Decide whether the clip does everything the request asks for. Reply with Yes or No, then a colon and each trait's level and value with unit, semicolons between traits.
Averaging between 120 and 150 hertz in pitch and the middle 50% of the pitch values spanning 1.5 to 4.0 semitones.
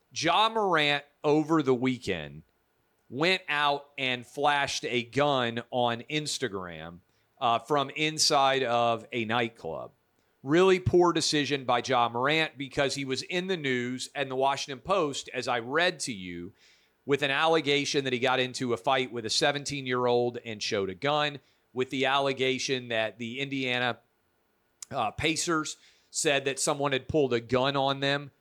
Yes: low, 135 Hz; average, 3.3 semitones